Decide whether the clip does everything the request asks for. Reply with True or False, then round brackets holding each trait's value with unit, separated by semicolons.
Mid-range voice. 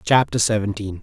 False (105 Hz)